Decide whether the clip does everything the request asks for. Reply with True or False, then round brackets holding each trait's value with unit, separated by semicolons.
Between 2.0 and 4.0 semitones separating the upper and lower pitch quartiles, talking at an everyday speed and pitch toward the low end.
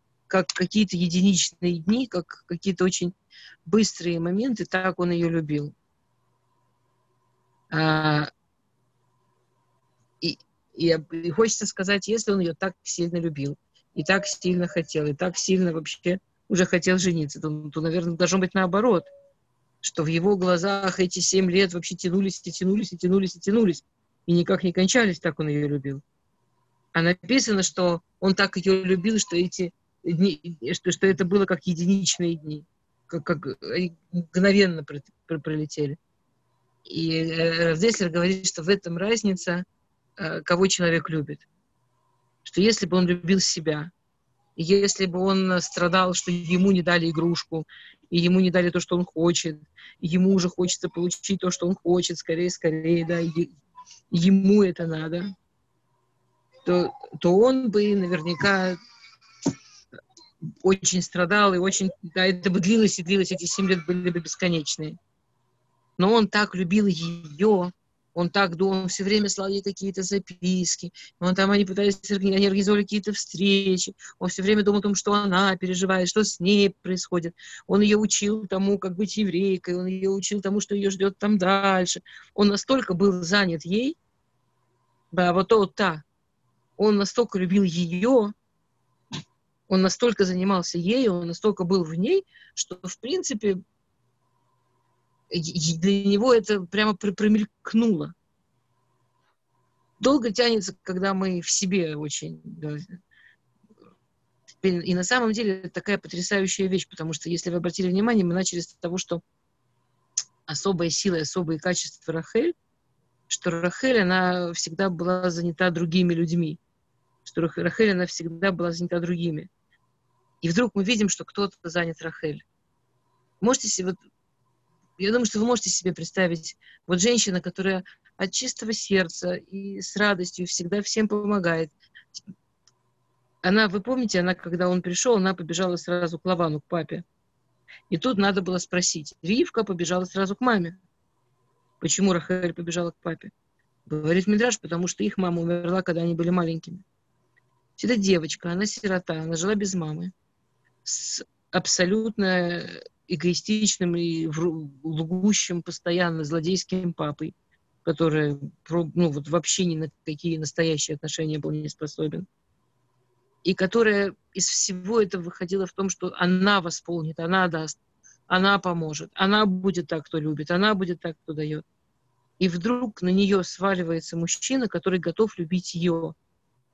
False (2.6 semitones; 145 wpm; 180 Hz)